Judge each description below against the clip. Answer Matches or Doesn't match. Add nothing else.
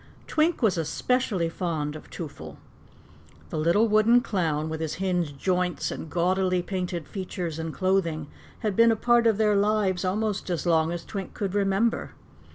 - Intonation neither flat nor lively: Matches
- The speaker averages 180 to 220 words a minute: Doesn't match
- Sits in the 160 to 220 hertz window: Matches